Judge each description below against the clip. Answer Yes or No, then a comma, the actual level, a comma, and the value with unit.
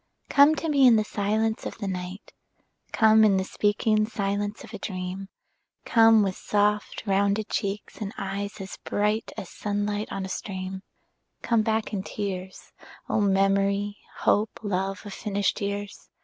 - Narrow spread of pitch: Yes, narrow, 1.7 semitones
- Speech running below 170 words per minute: Yes, average, 155 wpm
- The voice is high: Yes, high, 205 Hz